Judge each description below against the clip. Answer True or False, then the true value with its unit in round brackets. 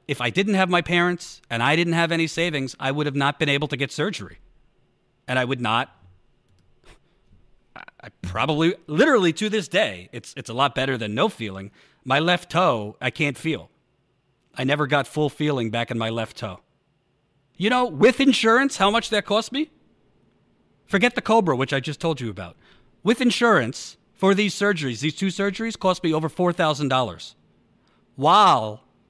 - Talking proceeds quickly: False (180 wpm)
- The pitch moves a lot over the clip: True (7.2 semitones)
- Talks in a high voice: False (150 Hz)